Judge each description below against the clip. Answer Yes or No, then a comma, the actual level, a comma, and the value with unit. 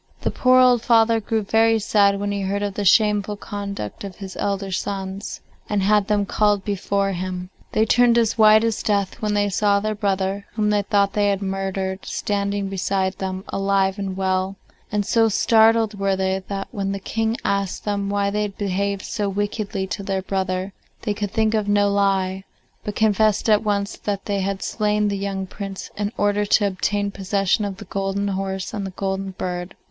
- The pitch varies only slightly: Yes, narrow, 1.4 semitones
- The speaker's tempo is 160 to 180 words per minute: No, average, 195 wpm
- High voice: Yes, high, 200 Hz